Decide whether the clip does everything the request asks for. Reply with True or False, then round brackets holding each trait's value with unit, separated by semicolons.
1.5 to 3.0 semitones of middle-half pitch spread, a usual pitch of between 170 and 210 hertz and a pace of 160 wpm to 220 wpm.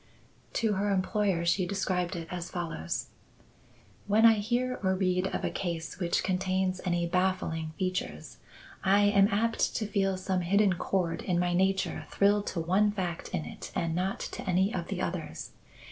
True (2.4 semitones; 185 Hz; 170 wpm)